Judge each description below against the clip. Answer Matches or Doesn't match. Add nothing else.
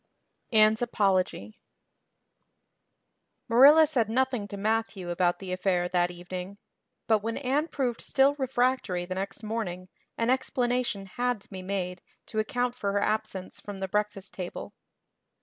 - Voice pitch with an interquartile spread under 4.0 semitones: Doesn't match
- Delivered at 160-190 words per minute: Doesn't match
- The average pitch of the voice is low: Doesn't match